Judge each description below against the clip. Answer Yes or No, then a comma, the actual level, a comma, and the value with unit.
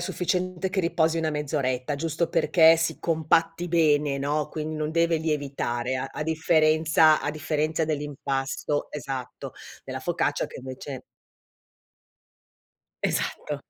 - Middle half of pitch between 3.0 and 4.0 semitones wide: No, narrow, 2.4 semitones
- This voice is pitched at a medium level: Yes, medium, 155 Hz